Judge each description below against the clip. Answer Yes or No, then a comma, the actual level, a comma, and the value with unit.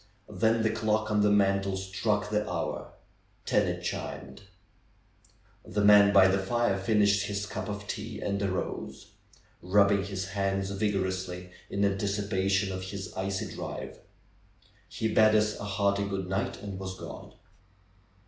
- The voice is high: No, low, 100 Hz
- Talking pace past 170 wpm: No, average, 145 wpm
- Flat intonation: Yes, narrow, 1.4 semitones